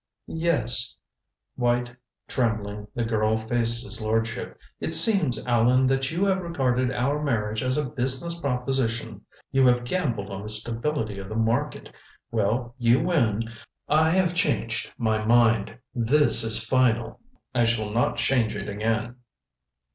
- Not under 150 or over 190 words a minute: No, average, 140 wpm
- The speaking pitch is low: Yes, low, 120 Hz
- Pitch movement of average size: Yes, average, 3.1 semitones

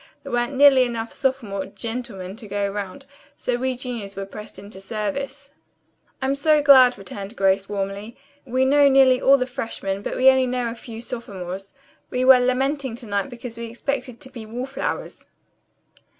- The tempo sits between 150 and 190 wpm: Yes, average, 175 wpm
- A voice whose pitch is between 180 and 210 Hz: No, high, 240 Hz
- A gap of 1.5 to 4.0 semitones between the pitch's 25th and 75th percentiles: No, average, 4.5 semitones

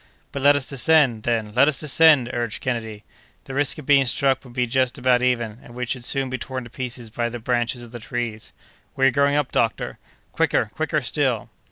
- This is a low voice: Yes, low, 125 Hz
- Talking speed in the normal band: No, fast, 215 wpm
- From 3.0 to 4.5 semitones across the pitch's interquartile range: No, narrow, 2.4 semitones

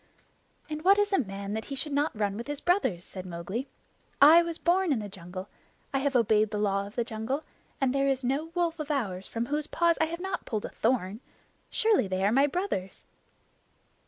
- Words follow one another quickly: Yes, fast, 215 wpm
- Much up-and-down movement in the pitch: Yes, wide, 7.3 semitones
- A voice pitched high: Yes, very high, 260 Hz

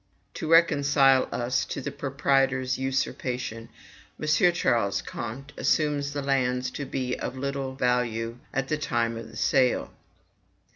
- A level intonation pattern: Yes, narrow, 2.2 semitones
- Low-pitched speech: Yes, low, 130 Hz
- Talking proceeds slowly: Yes, slow, 130 wpm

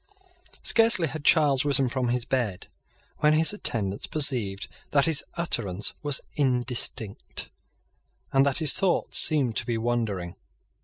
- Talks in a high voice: No, low, 130 Hz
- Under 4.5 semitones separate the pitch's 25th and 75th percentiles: No, average, 4.8 semitones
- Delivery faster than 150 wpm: No, slow, 135 wpm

